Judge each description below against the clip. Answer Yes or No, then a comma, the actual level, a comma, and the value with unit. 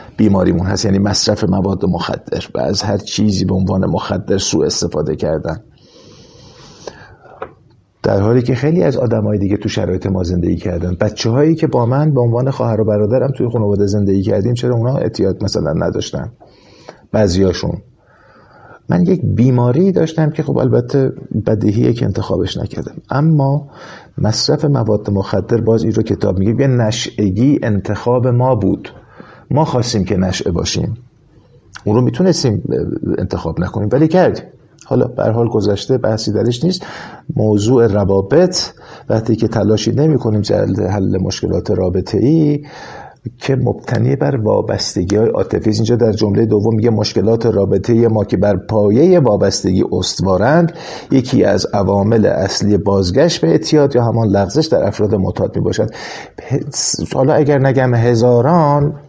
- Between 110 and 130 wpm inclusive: No, average, 140 wpm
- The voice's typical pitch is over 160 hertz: No, low, 115 Hz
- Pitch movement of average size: Yes, average, 4.6 semitones